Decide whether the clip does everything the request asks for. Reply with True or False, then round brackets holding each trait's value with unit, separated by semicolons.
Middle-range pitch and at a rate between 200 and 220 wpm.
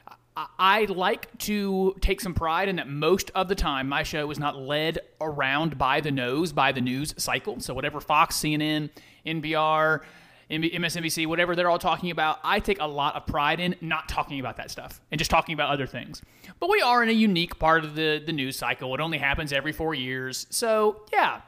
True (155 Hz; 205 wpm)